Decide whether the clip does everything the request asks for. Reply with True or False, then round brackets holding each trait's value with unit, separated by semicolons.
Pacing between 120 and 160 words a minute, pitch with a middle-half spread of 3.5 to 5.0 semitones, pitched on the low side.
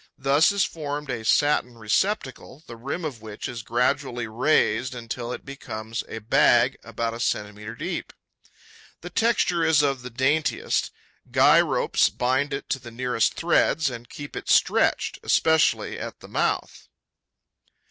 True (145 wpm; 3.9 semitones; 125 Hz)